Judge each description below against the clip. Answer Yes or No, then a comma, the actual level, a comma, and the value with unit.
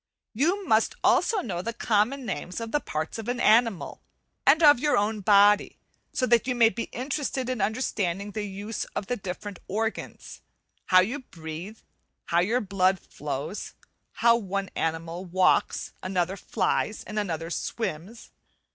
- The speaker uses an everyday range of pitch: Yes, average, 4.4 semitones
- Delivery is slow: No, average, 155 wpm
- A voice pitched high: Yes, high, 210 Hz